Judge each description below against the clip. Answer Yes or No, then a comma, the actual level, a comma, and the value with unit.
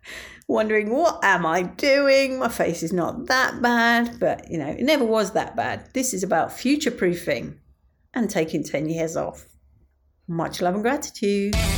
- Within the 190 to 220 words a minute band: No, average, 170 wpm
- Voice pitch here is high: Yes, high, 210 Hz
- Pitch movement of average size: No, wide, 7.5 semitones